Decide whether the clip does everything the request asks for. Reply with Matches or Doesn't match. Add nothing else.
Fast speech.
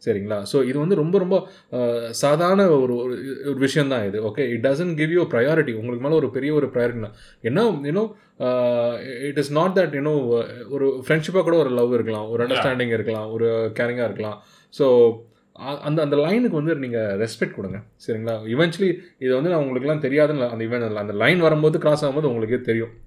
Matches